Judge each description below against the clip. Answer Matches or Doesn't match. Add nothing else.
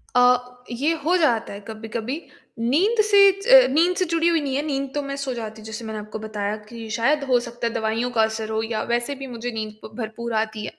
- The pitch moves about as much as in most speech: Matches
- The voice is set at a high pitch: Matches